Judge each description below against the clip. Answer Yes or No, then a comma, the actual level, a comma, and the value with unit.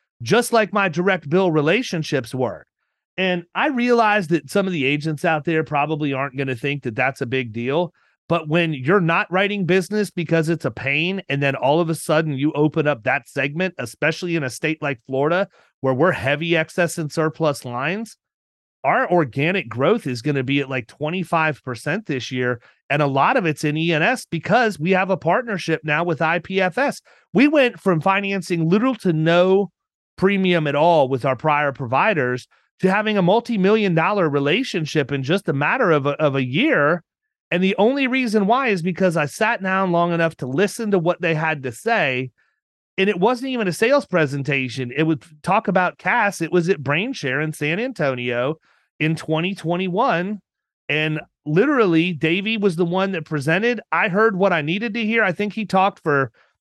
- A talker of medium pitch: Yes, medium, 165 Hz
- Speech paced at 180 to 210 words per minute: Yes, average, 190 wpm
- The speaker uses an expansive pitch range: No, average, 4.8 semitones